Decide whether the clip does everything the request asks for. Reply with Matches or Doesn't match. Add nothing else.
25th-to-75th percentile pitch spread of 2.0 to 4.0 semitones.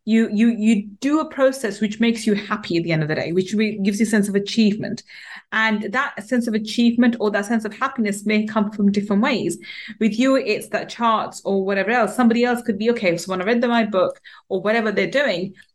Matches